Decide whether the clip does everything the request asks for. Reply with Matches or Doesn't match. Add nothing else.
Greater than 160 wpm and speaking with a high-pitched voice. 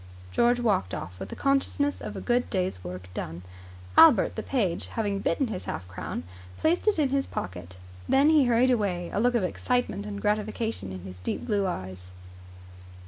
Matches